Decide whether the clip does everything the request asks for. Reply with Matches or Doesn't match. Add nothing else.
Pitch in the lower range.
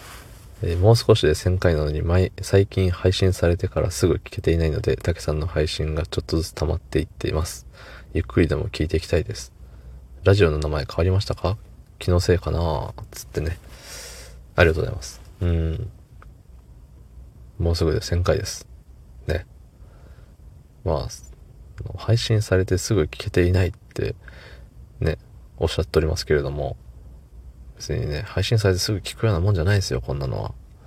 Matches